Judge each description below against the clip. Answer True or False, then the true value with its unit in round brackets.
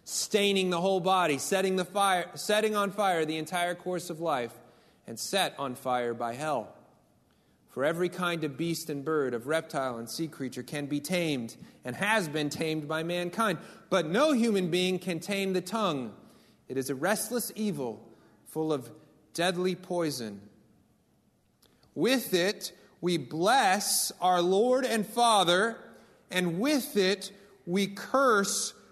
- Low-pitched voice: False (175 Hz)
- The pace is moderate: True (150 wpm)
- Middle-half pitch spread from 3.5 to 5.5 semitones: True (4.8 semitones)